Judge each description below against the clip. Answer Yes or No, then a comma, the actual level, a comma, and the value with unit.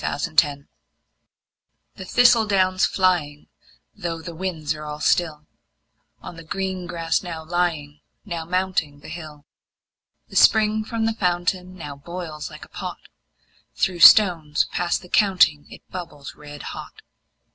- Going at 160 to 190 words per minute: No, slow, 135 wpm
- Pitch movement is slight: No, average, 3.5 semitones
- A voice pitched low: No, medium, 175 Hz